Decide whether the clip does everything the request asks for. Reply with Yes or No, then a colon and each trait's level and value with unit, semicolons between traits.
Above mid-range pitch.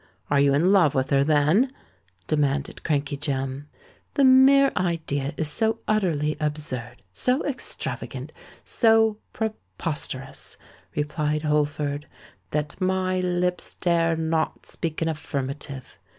No: medium, 155 Hz